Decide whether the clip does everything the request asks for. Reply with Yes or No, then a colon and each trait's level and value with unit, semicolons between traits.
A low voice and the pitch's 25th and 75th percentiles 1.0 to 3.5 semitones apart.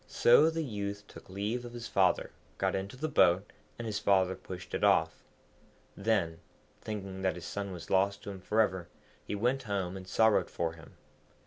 Yes: low, 100 Hz; average, 3.0 semitones